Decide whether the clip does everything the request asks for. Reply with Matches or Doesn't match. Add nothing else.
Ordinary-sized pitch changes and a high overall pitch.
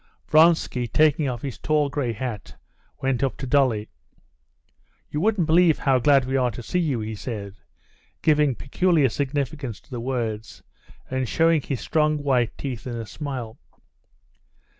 Doesn't match